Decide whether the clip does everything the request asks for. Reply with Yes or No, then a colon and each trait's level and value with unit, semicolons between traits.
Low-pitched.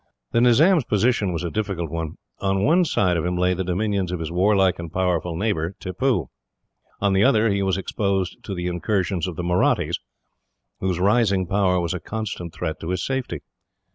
Yes: very low, 95 Hz